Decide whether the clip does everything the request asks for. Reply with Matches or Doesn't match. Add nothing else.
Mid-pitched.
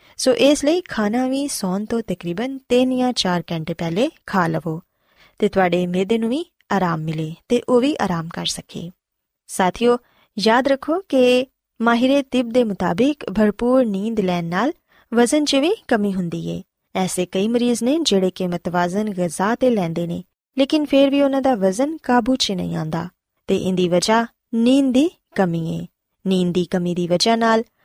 Doesn't match